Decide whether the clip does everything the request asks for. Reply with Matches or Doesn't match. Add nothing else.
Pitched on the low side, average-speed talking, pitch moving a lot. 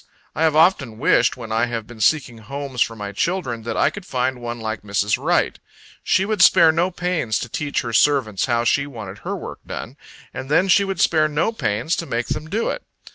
Doesn't match